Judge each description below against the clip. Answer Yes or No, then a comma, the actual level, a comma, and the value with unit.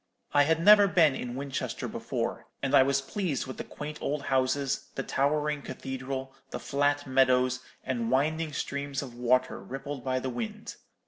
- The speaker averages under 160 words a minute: No, average, 170 wpm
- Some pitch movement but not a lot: No, narrow, 1.9 semitones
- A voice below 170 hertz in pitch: Yes, low, 135 Hz